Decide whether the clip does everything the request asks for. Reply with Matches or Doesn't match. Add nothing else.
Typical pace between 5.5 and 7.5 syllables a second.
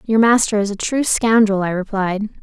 Doesn't match